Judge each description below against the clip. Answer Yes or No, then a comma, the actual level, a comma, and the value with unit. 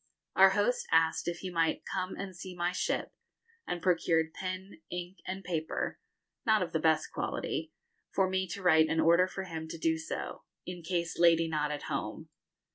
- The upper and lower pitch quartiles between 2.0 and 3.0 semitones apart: Yes, narrow, 2.4 semitones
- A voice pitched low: No, medium, 175 Hz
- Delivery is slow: No, average, 180 wpm